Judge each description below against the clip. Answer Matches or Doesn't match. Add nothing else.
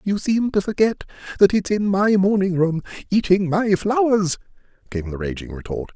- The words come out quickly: Doesn't match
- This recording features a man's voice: Matches